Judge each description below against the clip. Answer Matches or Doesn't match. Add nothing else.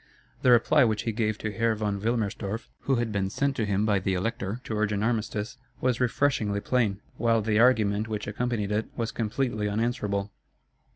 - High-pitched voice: Doesn't match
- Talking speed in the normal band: Matches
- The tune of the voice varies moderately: Doesn't match